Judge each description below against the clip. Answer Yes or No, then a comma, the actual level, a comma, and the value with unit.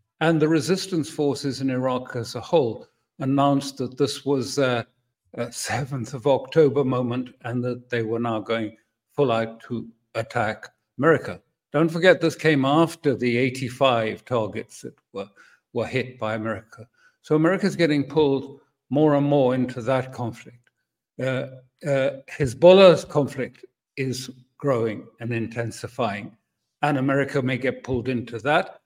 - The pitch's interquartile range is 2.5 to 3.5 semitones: Yes, average, 3.1 semitones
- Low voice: Yes, low, 130 Hz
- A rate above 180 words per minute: No, average, 145 wpm